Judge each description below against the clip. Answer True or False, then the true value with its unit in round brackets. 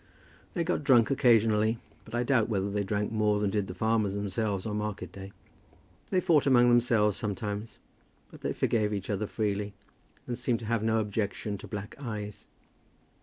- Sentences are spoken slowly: False (175 wpm)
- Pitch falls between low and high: False (110 Hz)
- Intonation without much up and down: True (2.3 semitones)